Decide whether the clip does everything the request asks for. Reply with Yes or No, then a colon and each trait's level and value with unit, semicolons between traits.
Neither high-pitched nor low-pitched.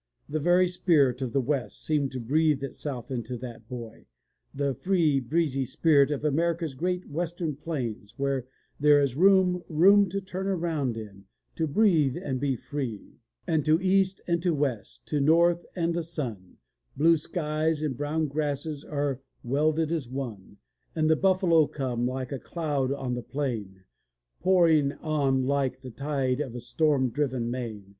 Yes: medium, 145 Hz